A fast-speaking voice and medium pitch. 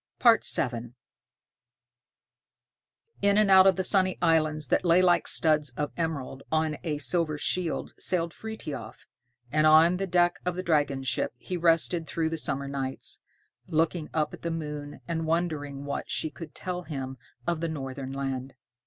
No: average, 160 wpm; medium, 160 Hz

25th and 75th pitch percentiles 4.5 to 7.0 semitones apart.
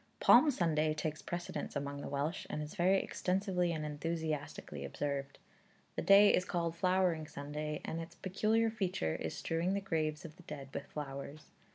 No: average, 3.6 semitones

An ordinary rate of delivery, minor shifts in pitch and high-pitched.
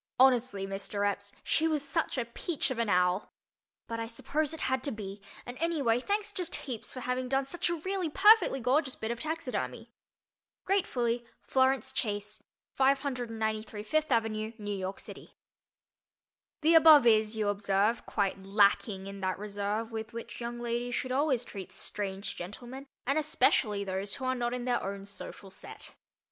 No: average, 165 wpm; average, 4.7 semitones; high, 235 Hz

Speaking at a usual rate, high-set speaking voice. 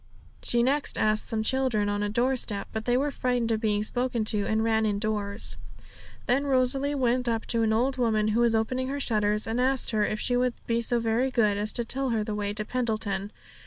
No: fast, 220 wpm; high, 230 Hz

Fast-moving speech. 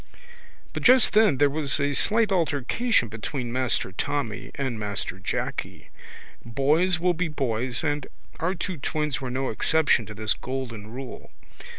No: average, 150 wpm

